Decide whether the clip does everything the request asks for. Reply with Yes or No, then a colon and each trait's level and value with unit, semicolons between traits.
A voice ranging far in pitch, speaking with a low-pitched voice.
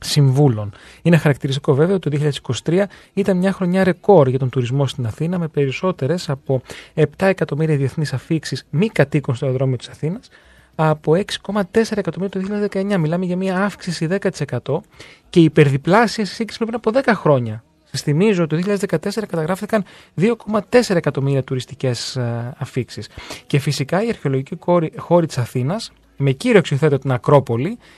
No: wide, 6.0 semitones; medium, 155 Hz